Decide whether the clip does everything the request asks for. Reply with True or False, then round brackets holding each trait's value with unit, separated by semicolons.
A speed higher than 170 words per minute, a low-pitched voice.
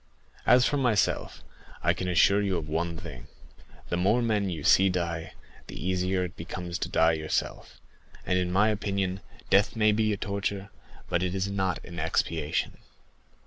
False (165 wpm; 95 Hz)